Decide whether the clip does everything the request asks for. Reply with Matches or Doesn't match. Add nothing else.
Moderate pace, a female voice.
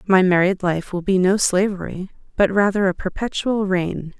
Matches